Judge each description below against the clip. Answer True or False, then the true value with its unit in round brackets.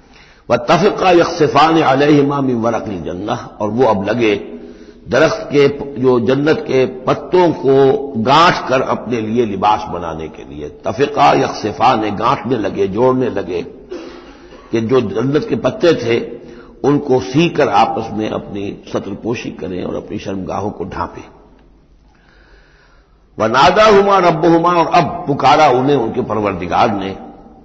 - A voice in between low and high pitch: False (130 Hz)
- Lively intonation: True (6.1 semitones)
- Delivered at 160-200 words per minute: False (140 wpm)